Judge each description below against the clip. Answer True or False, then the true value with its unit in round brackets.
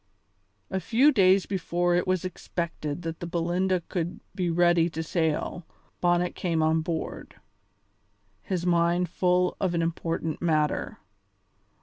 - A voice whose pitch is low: False (175 Hz)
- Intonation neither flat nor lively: False (1.7 semitones)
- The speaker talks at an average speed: False (130 wpm)